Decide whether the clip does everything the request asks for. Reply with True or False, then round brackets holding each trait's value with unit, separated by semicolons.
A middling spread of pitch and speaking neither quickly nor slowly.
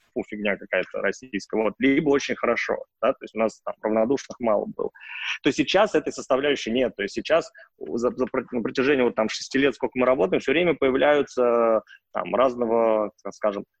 False (3.6 semitones; 185 wpm)